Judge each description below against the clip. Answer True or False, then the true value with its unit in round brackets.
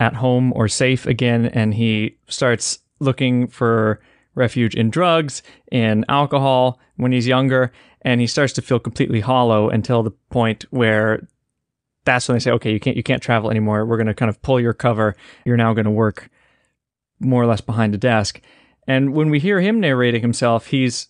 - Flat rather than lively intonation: True (2.3 semitones)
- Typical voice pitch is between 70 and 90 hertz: False (120 Hz)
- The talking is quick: False (185 wpm)